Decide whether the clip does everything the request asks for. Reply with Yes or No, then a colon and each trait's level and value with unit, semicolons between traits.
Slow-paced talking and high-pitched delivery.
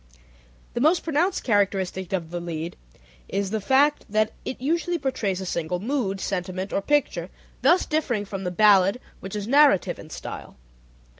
No: average, 160 wpm; high, 205 Hz